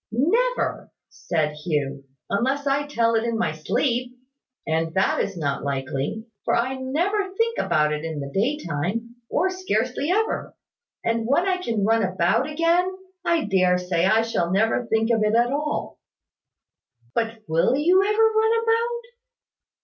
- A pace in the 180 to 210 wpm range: No, average, 155 wpm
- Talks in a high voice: Yes, high, 230 Hz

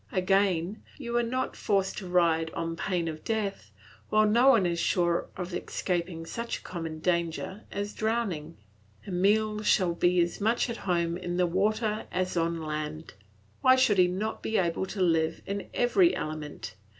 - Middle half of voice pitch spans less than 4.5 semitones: Yes, average, 4.1 semitones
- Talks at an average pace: Yes, average, 170 wpm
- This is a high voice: No, medium, 180 Hz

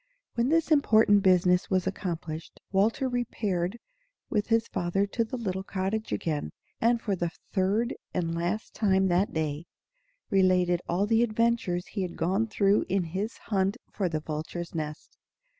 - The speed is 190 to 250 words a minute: No, average, 155 wpm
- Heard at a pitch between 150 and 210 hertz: Yes, high, 190 Hz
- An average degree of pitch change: Yes, average, 3.9 semitones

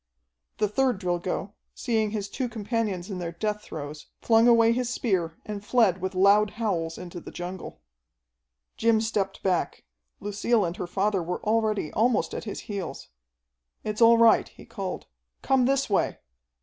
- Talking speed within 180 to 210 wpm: No, average, 160 wpm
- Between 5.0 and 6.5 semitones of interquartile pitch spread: No, average, 3.8 semitones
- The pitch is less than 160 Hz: No, high, 210 Hz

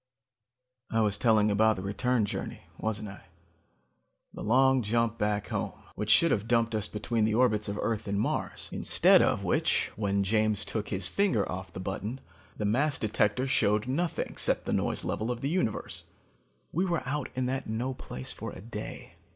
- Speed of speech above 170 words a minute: Yes, average, 185 wpm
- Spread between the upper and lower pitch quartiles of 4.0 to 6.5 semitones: No, average, 3.3 semitones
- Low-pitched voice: Yes, low, 110 Hz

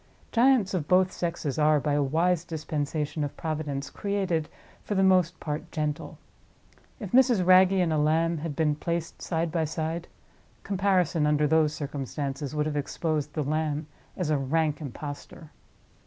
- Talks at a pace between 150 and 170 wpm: Yes, average, 155 wpm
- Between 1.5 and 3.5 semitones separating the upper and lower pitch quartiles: Yes, average, 3.0 semitones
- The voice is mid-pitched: Yes, medium, 160 Hz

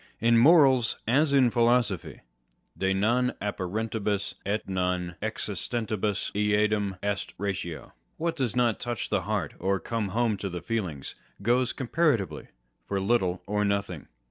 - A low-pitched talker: Yes, low, 105 Hz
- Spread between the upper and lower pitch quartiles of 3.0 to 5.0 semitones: Yes, average, 3.8 semitones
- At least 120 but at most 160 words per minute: Yes, average, 145 wpm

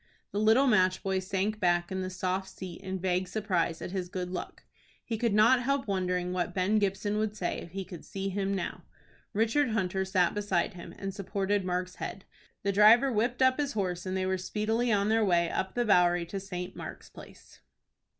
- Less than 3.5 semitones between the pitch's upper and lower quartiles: Yes, average, 2.7 semitones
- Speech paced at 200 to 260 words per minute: Yes, fast, 205 wpm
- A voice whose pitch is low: No, high, 195 Hz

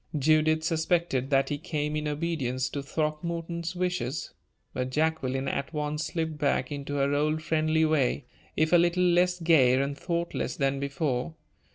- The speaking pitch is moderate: Yes, medium, 155 Hz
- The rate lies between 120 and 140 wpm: No, average, 155 wpm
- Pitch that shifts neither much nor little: Yes, average, 3.0 semitones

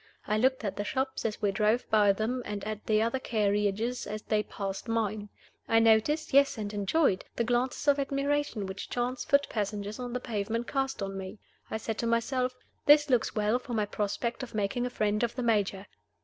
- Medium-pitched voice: No, high, 225 Hz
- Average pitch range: Yes, average, 3.3 semitones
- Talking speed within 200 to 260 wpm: Yes, fast, 205 wpm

